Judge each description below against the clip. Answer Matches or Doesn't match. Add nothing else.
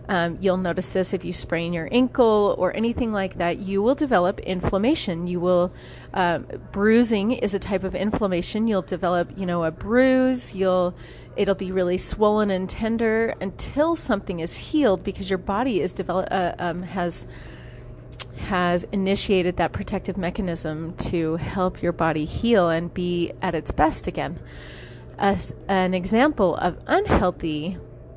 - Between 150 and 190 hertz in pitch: Matches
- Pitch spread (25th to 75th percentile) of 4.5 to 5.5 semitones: Doesn't match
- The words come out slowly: Doesn't match